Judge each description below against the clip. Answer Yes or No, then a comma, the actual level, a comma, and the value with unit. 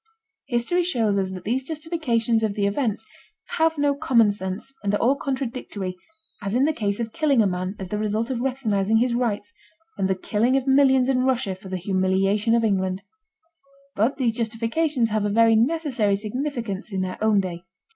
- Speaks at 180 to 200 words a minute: Yes, average, 185 wpm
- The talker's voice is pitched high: Yes, high, 225 Hz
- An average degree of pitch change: Yes, average, 4.7 semitones